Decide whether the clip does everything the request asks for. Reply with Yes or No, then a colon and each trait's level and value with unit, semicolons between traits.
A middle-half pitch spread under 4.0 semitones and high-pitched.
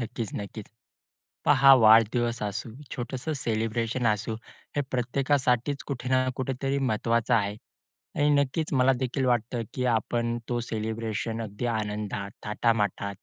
No: average, 3.0 semitones; low, 115 Hz